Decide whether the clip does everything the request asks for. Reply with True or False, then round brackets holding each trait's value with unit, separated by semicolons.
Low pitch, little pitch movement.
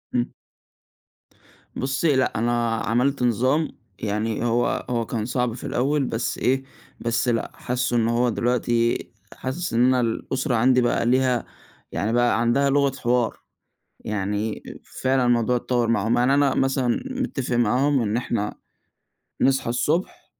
True (120 Hz; 2.2 semitones)